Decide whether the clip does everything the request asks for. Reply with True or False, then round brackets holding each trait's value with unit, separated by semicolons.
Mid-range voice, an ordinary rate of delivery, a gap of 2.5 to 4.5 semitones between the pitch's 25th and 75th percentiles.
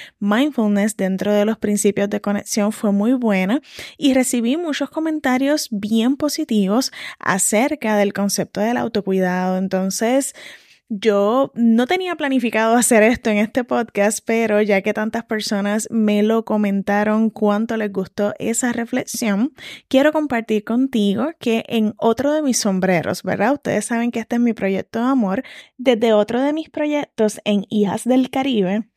False (225 Hz; 150 wpm; 3.7 semitones)